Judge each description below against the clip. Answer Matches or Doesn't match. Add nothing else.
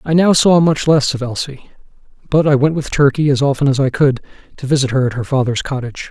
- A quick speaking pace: Matches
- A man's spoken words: Matches